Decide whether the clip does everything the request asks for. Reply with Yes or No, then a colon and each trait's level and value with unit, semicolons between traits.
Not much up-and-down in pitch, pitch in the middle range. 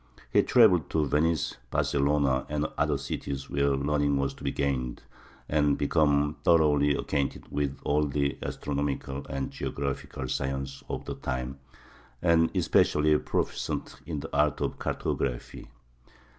No: narrow, 1.5 semitones; very low, 70 Hz